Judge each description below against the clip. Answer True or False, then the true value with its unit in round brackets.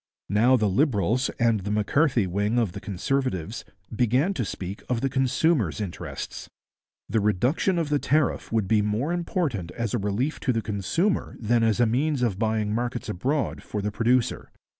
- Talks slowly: False (175 wpm)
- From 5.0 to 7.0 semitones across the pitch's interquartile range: False (4.3 semitones)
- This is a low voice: True (115 Hz)